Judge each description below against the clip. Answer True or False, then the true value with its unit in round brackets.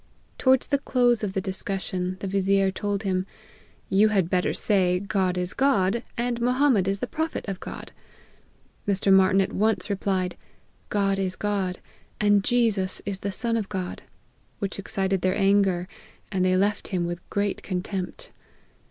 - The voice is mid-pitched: False (195 Hz)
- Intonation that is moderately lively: False (2.0 semitones)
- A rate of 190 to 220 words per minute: False (170 wpm)